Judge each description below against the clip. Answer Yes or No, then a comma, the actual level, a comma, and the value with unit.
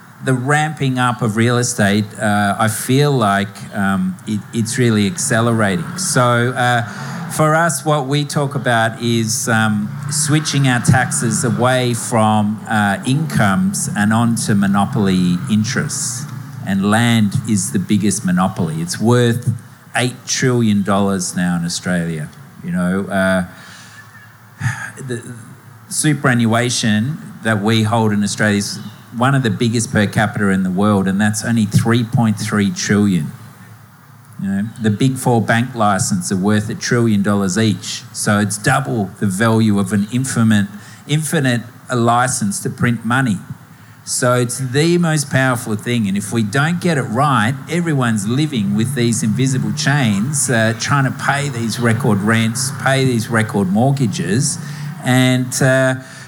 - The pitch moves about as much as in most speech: Yes, average, 3.9 semitones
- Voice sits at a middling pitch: No, low, 115 Hz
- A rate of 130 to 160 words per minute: Yes, average, 140 wpm